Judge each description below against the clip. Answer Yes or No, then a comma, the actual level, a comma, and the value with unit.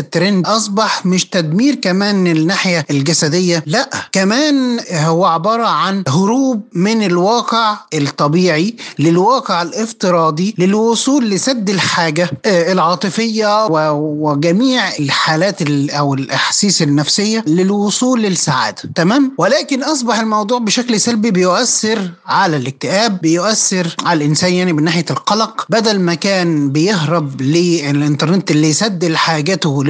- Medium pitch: Yes, medium, 180 Hz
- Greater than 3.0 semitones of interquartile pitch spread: Yes, average, 5.1 semitones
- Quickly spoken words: No, average, 105 wpm